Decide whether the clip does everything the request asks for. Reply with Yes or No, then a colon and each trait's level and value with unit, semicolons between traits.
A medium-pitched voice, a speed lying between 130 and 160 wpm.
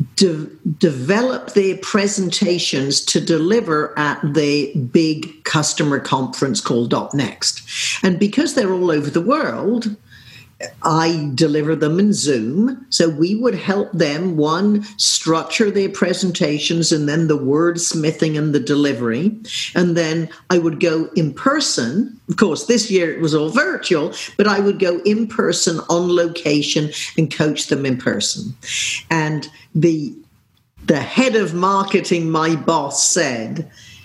Yes: medium, 170 Hz; average, 140 wpm